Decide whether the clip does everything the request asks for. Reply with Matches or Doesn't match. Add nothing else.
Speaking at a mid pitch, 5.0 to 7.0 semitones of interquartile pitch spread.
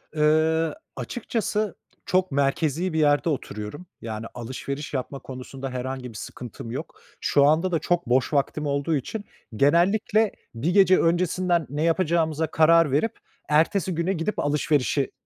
Doesn't match